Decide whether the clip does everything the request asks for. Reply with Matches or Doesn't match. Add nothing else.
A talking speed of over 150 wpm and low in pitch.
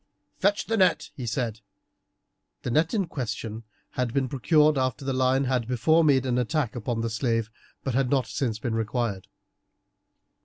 Matches